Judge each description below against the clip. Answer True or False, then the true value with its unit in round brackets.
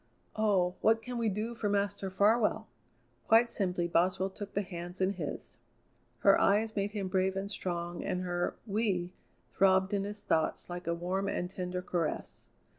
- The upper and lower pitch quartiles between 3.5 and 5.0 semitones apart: False (2.4 semitones)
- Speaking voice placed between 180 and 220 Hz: True (190 Hz)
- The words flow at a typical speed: True (170 wpm)